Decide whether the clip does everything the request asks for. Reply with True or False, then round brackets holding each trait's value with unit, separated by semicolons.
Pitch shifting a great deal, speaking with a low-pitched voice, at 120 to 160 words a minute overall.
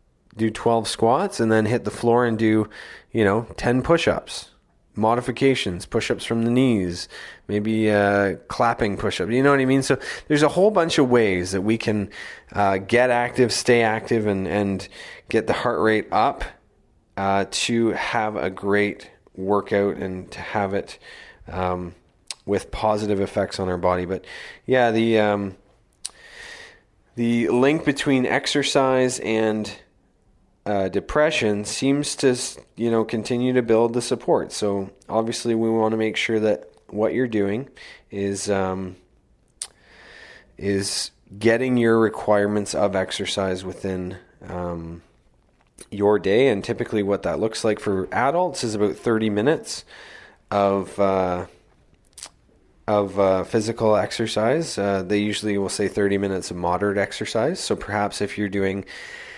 False (3.1 semitones; 105 Hz; 145 wpm)